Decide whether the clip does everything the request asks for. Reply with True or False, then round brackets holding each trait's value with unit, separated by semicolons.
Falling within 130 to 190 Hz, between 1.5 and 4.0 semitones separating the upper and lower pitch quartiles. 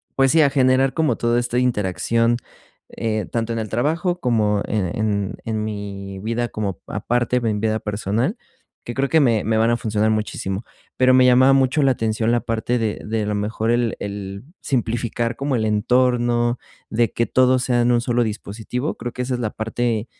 False (115 Hz; 2.6 semitones)